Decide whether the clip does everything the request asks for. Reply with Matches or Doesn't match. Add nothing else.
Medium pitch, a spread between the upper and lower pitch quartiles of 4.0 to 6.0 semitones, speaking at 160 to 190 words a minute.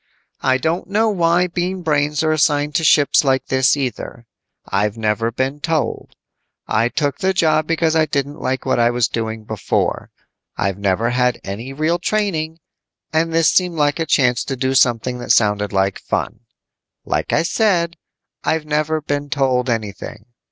Matches